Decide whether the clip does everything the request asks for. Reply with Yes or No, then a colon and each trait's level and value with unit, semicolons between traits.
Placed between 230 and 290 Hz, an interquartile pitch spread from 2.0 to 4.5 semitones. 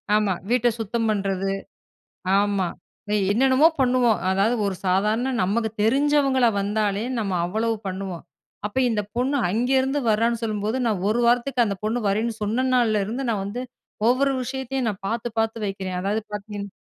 No: high, 220 Hz; average, 3.5 semitones